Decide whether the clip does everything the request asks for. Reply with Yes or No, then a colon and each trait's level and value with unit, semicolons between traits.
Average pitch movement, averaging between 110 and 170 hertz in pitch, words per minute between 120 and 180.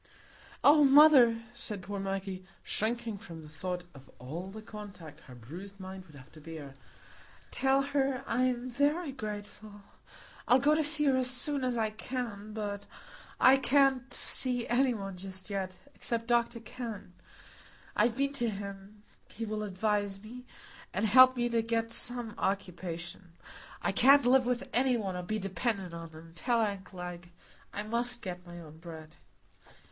No: average, 4.9 semitones; high, 215 Hz; average, 160 wpm